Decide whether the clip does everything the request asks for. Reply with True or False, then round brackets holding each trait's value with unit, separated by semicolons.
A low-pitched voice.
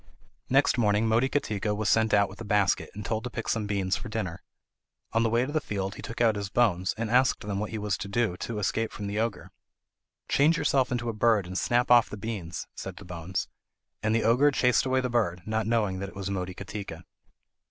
True (110 Hz)